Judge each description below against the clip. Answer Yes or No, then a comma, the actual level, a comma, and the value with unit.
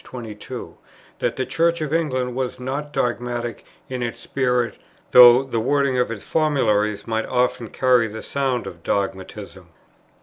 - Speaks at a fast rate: No, average, 155 wpm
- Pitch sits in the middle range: No, low, 125 Hz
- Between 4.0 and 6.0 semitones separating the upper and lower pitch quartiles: No, average, 2.9 semitones